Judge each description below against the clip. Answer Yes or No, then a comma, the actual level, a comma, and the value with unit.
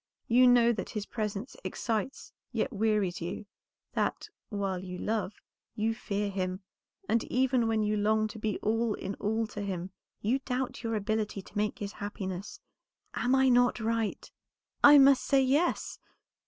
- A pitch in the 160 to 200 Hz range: No, high, 215 Hz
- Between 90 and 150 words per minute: No, average, 160 wpm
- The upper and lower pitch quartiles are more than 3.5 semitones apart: No, average, 3.1 semitones